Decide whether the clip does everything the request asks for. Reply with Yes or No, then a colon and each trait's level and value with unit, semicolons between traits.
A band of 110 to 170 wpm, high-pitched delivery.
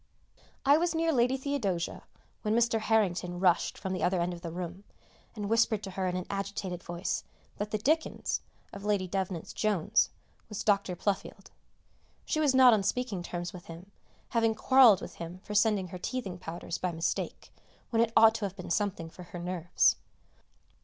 No: average, 180 wpm; high, 195 Hz